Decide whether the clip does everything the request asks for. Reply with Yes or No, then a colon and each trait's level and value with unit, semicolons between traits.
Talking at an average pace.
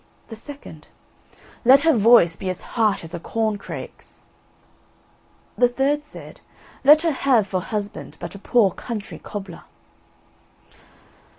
No: slow, 130 wpm